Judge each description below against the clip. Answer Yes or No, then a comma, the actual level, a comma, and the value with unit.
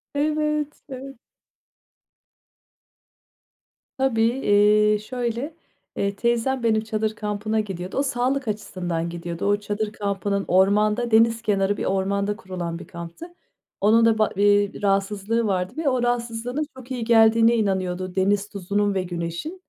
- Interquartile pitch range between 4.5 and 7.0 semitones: No, average, 3.2 semitones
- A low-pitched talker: No, high, 210 Hz